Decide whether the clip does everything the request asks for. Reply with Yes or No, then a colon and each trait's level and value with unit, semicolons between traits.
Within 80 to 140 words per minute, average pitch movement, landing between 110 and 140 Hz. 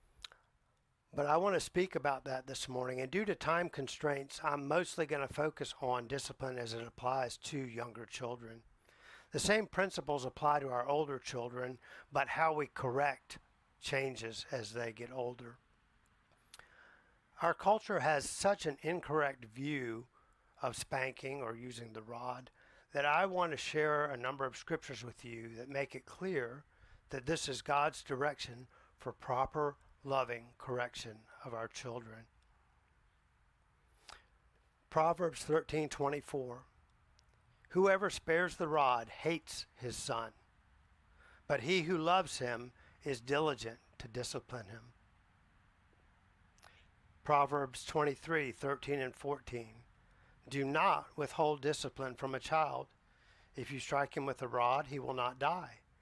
Yes: slow, 135 wpm; average, 3.8 semitones; low, 135 Hz